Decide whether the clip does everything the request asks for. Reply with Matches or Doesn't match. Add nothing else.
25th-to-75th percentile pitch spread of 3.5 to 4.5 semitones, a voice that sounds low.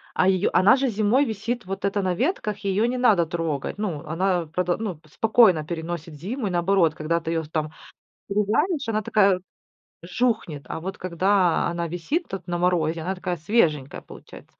Doesn't match